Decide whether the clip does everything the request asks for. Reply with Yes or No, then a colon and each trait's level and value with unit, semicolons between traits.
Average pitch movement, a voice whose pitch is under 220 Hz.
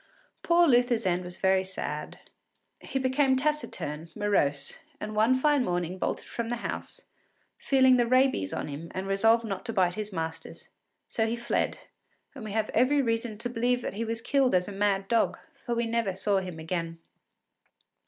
No: average, 4.6 semitones; high, 225 Hz